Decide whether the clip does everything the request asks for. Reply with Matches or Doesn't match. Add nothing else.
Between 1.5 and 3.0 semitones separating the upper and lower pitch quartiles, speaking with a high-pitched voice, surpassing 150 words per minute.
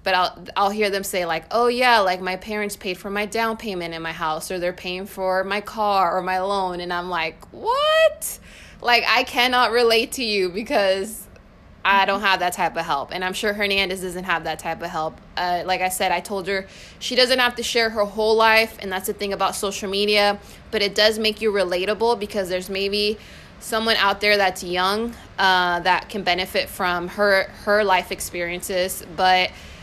Matches